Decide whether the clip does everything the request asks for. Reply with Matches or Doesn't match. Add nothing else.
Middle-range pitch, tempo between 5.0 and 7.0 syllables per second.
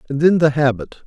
Matches